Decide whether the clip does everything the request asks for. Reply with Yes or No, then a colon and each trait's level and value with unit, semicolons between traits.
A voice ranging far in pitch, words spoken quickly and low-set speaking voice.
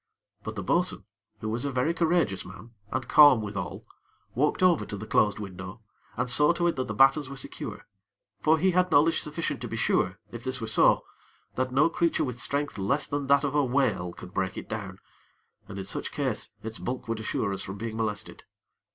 Yes: wide, 5.8 semitones; fast, 210 wpm; low, 125 Hz